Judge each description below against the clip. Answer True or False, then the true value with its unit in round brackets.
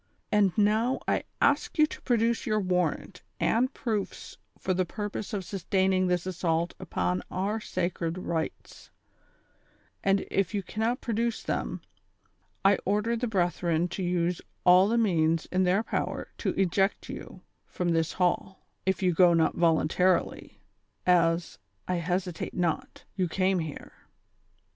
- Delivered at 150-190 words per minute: False (140 wpm)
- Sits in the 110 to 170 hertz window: False (185 Hz)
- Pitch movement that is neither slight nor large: True (3.1 semitones)